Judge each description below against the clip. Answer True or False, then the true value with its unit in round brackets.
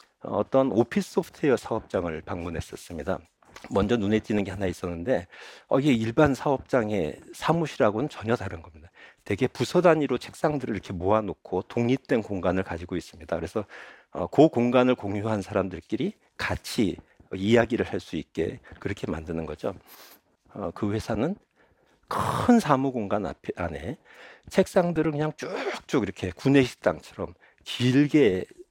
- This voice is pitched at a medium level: False (120 Hz)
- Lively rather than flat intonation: True (6.8 semitones)